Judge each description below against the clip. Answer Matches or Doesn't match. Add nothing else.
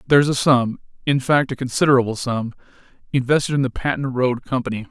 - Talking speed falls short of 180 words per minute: Matches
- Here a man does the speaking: Matches